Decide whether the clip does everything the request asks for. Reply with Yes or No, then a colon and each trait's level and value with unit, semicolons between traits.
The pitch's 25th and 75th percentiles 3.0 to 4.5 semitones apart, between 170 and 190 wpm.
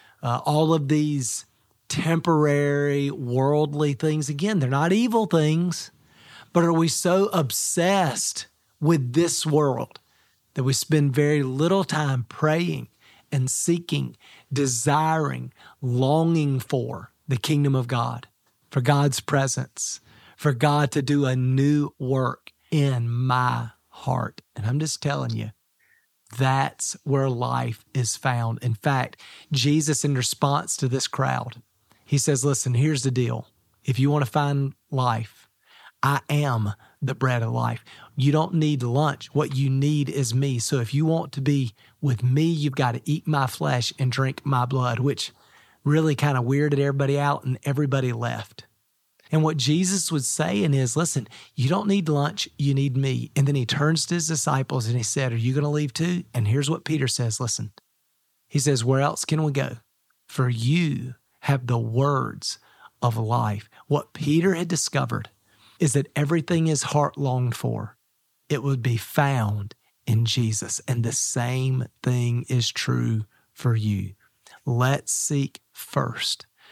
No: average, 3.4 semitones; average, 155 wpm